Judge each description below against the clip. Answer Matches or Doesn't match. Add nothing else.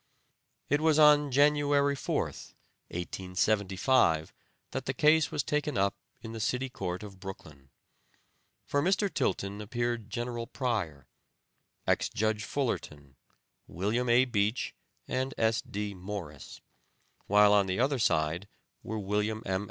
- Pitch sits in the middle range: Doesn't match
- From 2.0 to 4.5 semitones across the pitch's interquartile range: Doesn't match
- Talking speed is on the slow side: Matches